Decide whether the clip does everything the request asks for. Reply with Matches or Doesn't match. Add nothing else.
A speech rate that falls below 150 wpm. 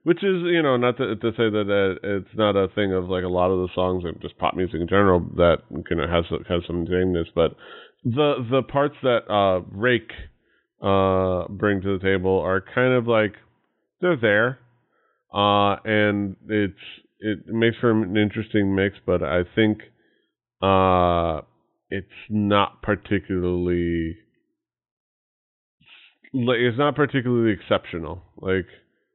Doesn't match